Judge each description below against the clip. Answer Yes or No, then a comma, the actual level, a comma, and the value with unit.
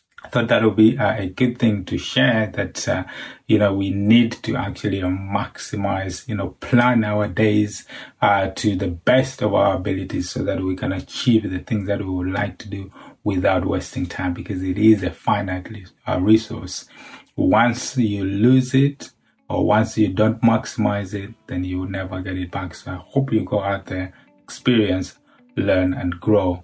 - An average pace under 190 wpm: Yes, average, 180 wpm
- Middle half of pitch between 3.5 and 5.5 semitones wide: No, average, 3.1 semitones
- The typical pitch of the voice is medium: No, low, 105 Hz